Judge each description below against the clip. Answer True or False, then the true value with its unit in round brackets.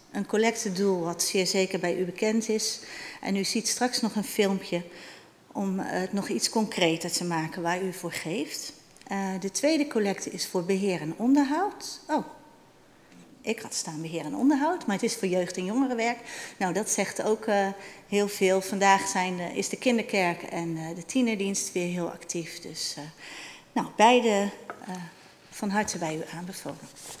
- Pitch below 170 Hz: False (195 Hz)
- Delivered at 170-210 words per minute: True (175 wpm)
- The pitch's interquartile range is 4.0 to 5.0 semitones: False (3.5 semitones)